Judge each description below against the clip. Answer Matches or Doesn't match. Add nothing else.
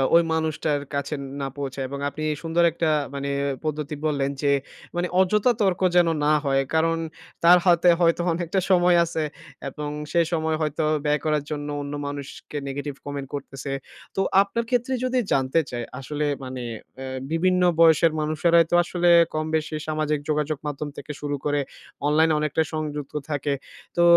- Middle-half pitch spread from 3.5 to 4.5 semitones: Doesn't match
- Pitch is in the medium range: Matches